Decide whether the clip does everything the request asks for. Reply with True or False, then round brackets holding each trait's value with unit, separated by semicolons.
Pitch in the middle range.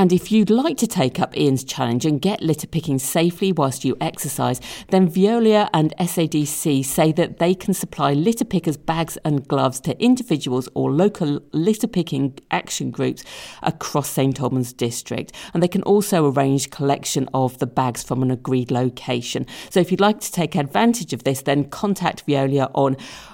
True (155 Hz)